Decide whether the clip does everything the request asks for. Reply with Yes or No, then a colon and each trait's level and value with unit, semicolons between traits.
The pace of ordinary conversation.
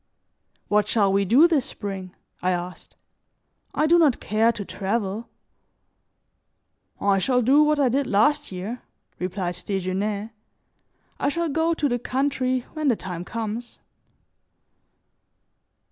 No: slow, 130 wpm